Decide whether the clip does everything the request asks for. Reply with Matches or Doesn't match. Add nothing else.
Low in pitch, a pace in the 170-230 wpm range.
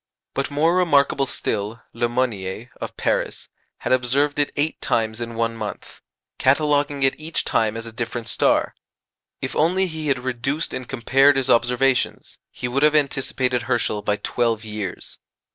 Doesn't match